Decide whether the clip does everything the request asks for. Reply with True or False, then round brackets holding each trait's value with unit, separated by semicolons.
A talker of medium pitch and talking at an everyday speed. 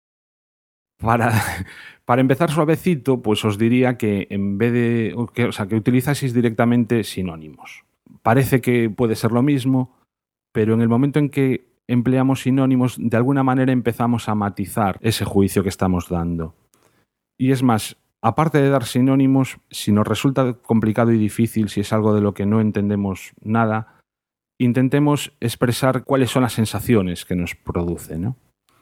False (115 Hz; 155 wpm)